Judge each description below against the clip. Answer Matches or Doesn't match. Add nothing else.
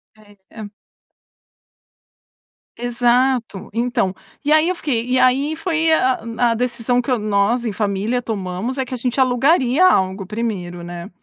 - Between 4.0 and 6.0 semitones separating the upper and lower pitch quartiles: Doesn't match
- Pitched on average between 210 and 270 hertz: Matches